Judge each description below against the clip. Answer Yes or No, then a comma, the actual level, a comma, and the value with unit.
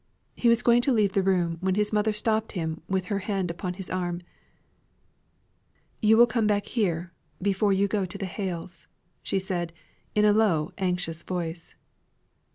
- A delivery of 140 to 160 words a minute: No, average, 170 wpm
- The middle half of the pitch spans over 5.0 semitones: No, average, 3.1 semitones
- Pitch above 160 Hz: Yes, high, 190 Hz